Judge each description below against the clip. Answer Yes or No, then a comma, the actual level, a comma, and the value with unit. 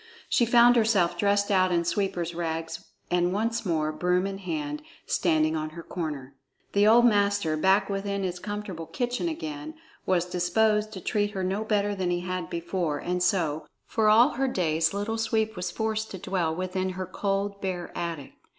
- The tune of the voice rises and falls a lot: No, average, 3.5 semitones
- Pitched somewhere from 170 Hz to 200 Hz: Yes, high, 190 Hz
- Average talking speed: Yes, average, 180 wpm